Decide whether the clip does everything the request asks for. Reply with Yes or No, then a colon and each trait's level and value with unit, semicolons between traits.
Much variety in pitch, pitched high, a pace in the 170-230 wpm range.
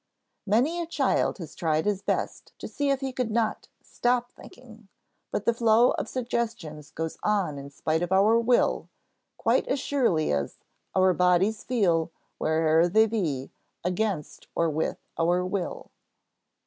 No: wide, 6.3 semitones; high, 200 Hz; average, 150 wpm